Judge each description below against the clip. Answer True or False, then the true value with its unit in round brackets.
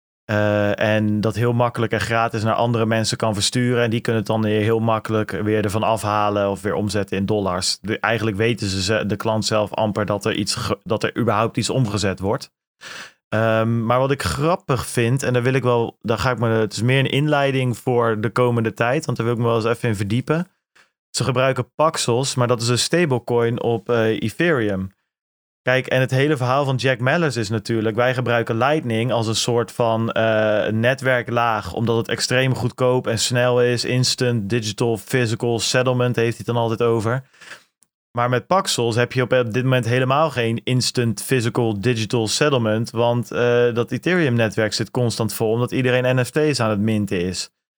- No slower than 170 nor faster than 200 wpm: True (195 wpm)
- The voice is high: False (115 Hz)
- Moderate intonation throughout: False (2.3 semitones)